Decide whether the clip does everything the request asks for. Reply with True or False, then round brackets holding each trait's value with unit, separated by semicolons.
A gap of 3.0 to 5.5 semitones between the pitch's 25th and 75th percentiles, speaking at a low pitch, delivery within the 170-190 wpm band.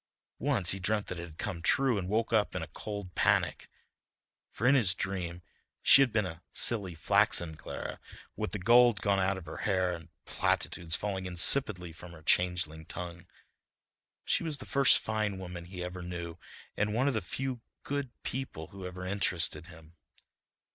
True (3.8 semitones; 95 Hz; 180 wpm)